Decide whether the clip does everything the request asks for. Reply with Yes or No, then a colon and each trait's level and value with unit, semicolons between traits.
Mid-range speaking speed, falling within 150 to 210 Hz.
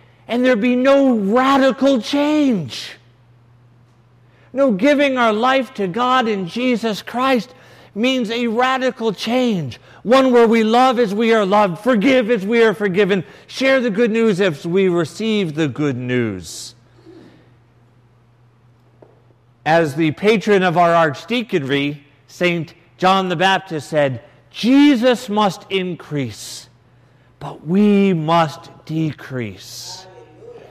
No: slow, 115 wpm; high, 190 Hz